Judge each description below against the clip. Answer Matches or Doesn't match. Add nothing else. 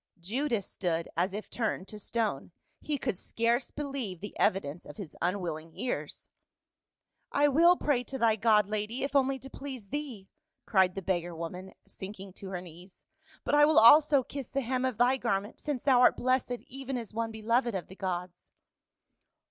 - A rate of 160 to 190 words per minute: Matches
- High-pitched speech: Matches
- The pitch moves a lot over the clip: Matches